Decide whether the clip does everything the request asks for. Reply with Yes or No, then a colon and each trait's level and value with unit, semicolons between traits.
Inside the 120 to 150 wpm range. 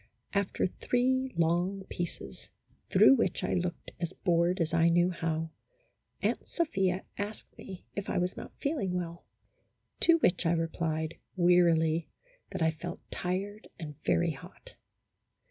Yes: average, 140 wpm